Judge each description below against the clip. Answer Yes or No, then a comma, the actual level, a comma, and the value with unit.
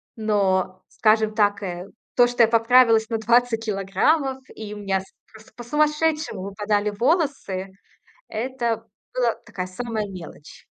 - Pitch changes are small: No, average, 3.4 semitones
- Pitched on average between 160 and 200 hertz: No, high, 220 Hz